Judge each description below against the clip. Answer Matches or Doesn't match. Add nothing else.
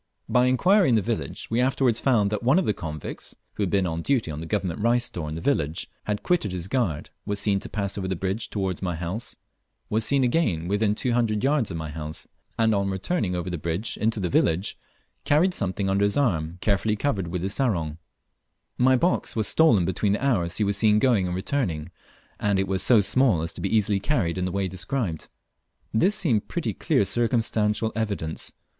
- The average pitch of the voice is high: Doesn't match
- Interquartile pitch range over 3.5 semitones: Matches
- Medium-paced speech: Doesn't match